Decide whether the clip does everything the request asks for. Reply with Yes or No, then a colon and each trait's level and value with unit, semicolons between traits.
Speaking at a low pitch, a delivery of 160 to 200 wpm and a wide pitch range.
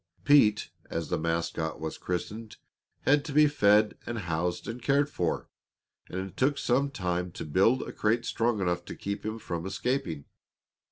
Yes: low, 105 Hz; average, 170 wpm; wide, 6.0 semitones